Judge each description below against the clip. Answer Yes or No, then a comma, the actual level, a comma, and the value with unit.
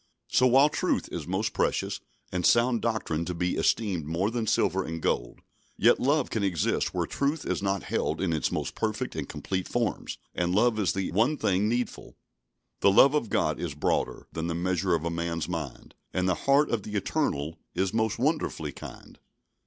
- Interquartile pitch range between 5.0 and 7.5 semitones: Yes, wide, 5.6 semitones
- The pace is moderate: Yes, average, 190 wpm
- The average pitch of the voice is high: No, very low, 95 Hz